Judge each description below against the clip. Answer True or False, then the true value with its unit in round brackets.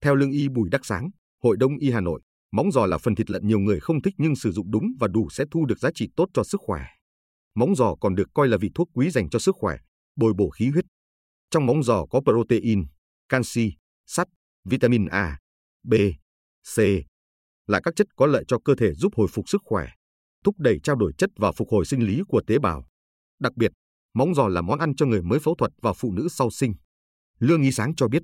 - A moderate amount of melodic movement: False (8.7 semitones)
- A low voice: True (115 Hz)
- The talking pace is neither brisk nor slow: True (240 wpm)